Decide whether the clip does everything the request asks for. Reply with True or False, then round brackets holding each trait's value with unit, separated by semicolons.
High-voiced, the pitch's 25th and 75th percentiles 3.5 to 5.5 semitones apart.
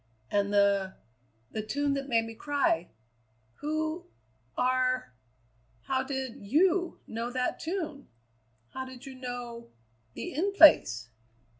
True (260 Hz; 4.2 semitones)